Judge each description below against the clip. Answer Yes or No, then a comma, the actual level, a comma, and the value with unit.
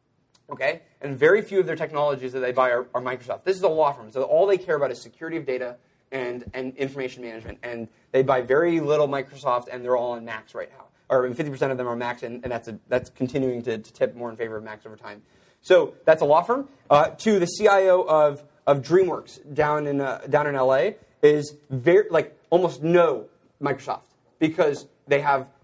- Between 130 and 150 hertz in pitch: Yes, low, 135 Hz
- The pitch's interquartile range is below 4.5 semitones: Yes, average, 4.1 semitones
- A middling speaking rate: No, fast, 220 wpm